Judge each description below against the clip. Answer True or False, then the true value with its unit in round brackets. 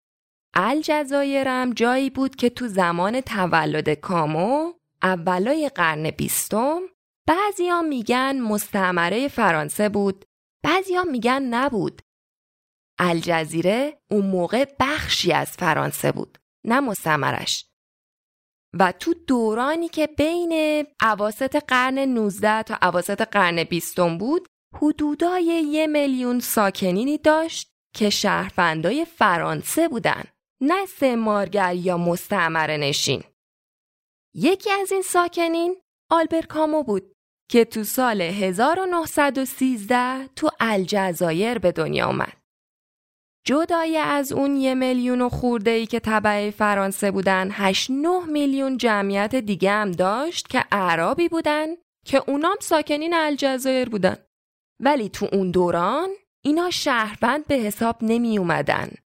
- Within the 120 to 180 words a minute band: False (110 wpm)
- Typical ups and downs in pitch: False (7.3 semitones)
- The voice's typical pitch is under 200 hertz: False (245 Hz)